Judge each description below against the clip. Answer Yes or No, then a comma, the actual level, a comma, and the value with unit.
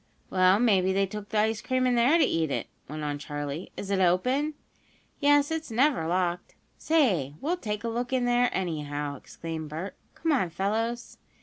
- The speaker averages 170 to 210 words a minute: Yes, average, 185 wpm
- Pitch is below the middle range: No, high, 205 Hz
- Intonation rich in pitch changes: Yes, wide, 7.0 semitones